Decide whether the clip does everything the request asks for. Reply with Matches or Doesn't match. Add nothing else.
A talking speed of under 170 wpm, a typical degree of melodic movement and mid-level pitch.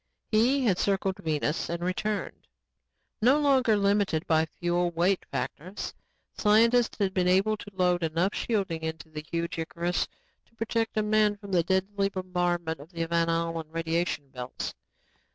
Matches